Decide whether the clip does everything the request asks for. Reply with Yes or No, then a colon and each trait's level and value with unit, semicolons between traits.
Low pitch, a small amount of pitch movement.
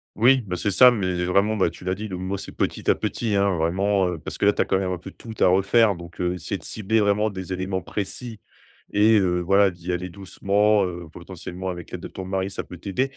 Yes: very low, 95 Hz; narrow, 2.3 semitones